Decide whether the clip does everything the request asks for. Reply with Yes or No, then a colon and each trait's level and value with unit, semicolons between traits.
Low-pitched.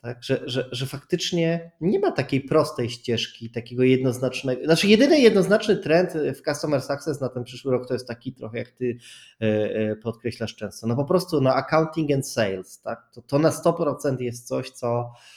Yes: low, 130 Hz